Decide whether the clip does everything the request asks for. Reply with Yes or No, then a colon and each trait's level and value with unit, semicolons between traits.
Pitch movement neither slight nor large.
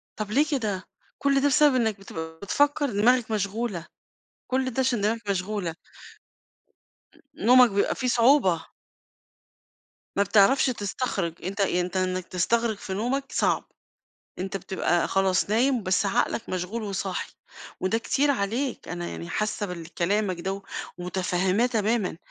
Yes: average, 4.5 semitones